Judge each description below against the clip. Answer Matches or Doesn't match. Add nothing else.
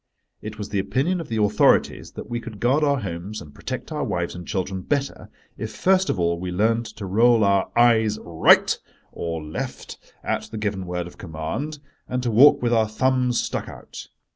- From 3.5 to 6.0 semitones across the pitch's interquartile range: Matches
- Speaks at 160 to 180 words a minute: Doesn't match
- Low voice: Matches